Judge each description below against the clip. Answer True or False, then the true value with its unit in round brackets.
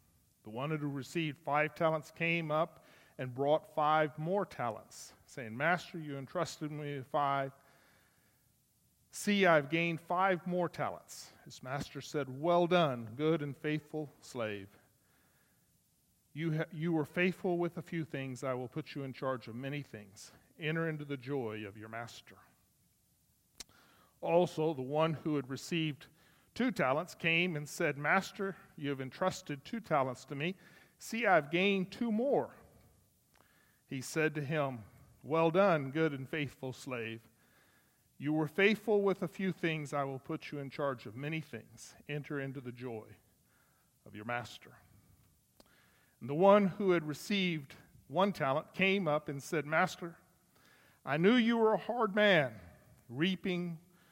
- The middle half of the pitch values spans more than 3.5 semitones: True (4.4 semitones)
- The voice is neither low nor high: True (155 Hz)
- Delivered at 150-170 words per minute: True (155 wpm)